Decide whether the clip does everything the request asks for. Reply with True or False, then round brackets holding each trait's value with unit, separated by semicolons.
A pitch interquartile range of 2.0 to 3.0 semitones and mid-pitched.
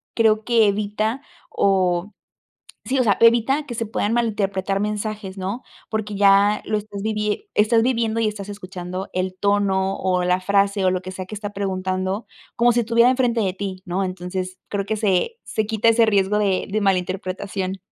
False (2.5 semitones; 205 Hz)